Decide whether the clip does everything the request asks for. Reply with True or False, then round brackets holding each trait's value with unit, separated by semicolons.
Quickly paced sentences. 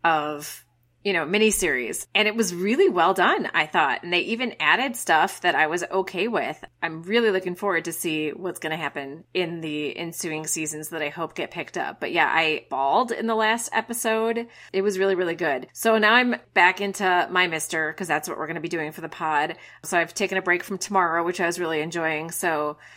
True (225 wpm)